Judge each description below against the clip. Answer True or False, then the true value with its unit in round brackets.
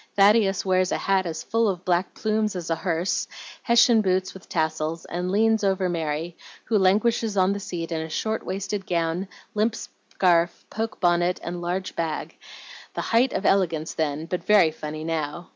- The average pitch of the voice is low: False (185 Hz)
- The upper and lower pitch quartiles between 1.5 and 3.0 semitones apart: False (3.4 semitones)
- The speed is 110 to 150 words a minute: False (175 wpm)